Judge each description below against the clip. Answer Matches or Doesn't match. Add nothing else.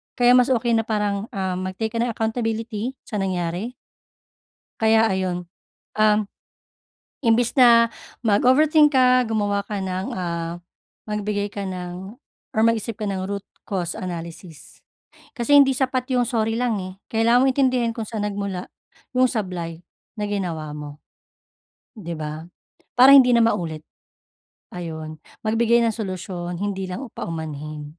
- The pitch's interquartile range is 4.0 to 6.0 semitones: Matches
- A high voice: Matches